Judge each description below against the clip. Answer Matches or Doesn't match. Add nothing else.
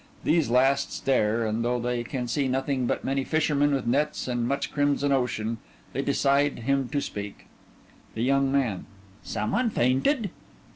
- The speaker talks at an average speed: Matches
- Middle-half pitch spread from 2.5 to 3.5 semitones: Matches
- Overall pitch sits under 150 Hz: Matches